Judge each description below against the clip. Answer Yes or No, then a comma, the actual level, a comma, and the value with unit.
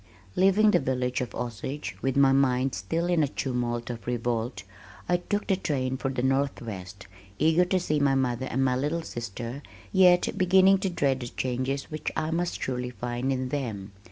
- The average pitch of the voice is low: Yes, low, 130 Hz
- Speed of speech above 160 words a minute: Yes, average, 185 wpm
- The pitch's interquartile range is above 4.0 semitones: Yes, average, 4.5 semitones